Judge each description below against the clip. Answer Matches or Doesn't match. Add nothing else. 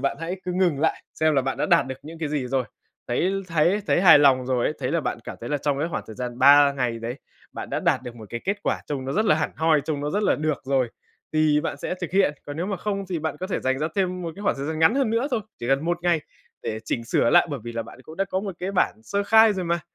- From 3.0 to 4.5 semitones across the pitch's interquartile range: Doesn't match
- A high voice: Doesn't match